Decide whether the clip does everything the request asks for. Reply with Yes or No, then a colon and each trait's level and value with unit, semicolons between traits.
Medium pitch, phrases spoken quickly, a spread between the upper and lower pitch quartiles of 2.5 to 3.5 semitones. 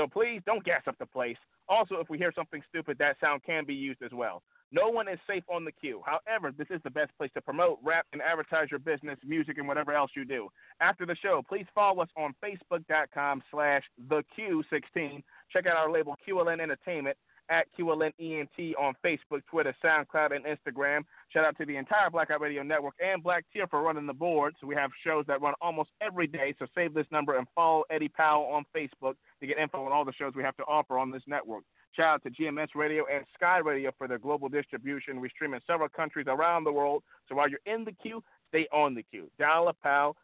Yes: medium, 155 Hz; fast, 230 wpm; average, 3.0 semitones